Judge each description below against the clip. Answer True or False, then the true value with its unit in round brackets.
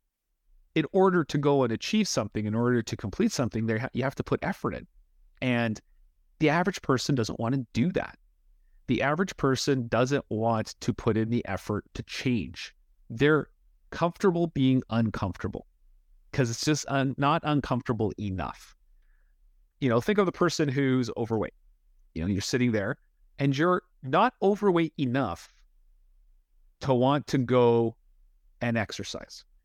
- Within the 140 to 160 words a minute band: True (150 wpm)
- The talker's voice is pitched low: True (125 Hz)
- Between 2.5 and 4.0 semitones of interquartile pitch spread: False (5.0 semitones)